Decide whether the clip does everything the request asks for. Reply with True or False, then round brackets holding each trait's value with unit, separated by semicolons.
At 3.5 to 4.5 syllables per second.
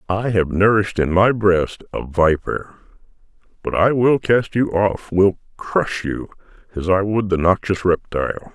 True (4.4 syllables/s)